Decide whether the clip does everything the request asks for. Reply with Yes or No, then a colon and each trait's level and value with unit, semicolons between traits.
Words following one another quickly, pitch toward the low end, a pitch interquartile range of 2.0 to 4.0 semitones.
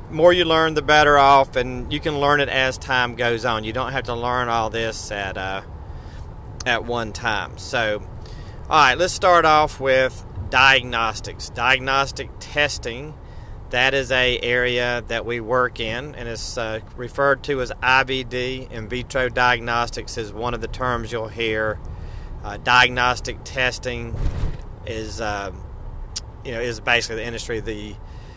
No: average, 155 wpm; low, 120 Hz; average, 3.0 semitones